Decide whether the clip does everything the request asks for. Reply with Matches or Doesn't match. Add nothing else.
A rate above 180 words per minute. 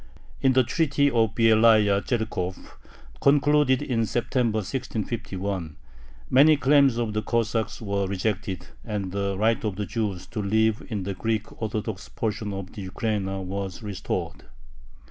Doesn't match